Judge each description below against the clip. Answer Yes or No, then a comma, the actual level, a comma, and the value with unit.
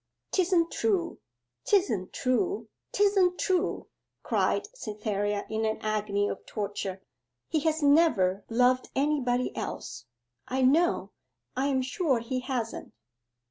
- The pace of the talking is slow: Yes, slow, 115 wpm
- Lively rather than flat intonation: Yes, wide, 7.8 semitones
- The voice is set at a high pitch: Yes, very high, 255 Hz